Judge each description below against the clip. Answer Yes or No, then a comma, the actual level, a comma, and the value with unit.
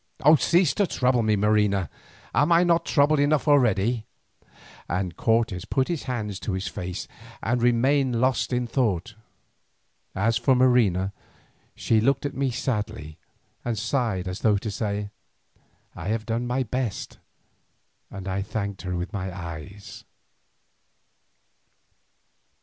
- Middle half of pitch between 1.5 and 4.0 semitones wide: No, average, 4.7 semitones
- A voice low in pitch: Yes, low, 110 Hz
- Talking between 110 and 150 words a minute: Yes, slow, 135 wpm